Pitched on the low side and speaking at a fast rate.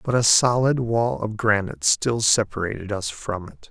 No: low, 105 Hz; average, 180 wpm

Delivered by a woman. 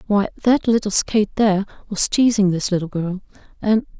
Yes: female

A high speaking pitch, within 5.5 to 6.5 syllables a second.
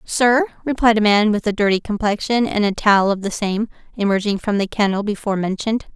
Yes: high, 210 Hz; 6.0 syllables/s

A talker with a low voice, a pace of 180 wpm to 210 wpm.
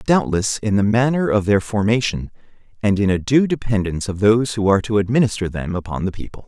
Yes: low, 105 Hz; fast, 205 wpm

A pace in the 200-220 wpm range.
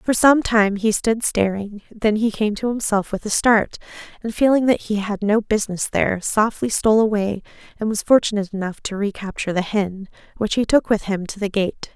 Yes: fast, 205 wpm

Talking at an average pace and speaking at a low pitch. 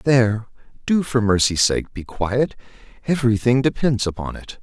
Yes: average, 155 wpm; low, 115 Hz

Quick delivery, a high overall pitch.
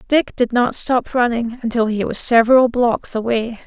No: average, 180 wpm; high, 240 Hz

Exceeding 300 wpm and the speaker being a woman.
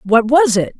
No: fast, 225 wpm; female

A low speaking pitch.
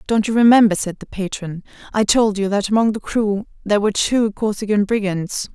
No: high, 210 Hz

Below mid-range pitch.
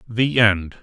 Yes: low, 110 Hz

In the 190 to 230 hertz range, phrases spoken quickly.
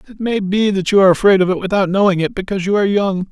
Yes: high, 195 Hz; fast, 290 wpm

